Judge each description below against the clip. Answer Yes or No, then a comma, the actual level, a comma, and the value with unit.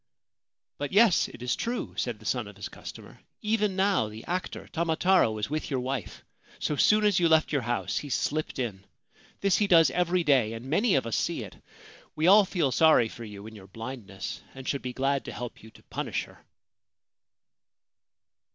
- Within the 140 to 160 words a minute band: No, average, 195 wpm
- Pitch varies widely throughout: Yes, wide, 7.4 semitones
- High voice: No, medium, 140 Hz